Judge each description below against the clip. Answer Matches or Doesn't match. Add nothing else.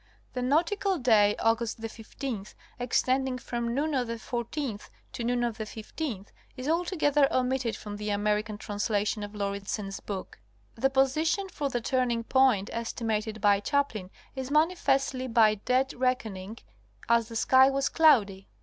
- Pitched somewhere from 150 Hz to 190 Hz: Doesn't match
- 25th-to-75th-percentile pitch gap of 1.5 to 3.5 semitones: Doesn't match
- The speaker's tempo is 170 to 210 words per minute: Doesn't match